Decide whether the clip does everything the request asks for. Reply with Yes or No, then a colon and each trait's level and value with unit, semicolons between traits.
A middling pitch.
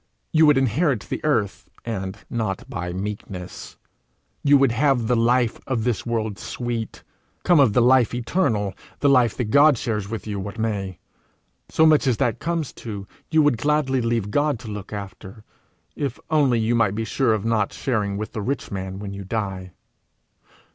No: low, 115 Hz